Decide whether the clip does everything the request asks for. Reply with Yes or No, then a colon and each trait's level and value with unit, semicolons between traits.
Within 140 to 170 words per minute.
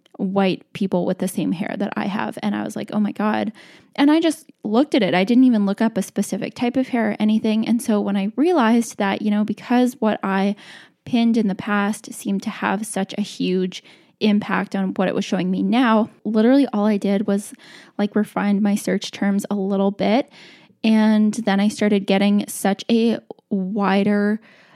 No: fast, 205 wpm